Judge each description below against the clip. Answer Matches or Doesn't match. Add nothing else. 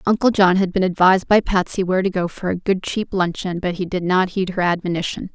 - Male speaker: Doesn't match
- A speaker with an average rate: Doesn't match